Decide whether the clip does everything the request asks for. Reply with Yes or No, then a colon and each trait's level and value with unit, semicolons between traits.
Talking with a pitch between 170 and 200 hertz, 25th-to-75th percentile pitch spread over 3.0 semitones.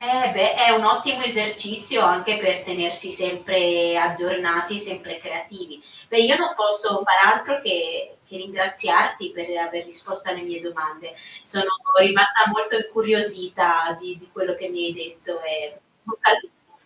Yes: high, 190 Hz; average, 3.9 semitones